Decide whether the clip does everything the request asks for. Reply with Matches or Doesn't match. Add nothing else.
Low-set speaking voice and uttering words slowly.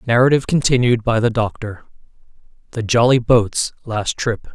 Matches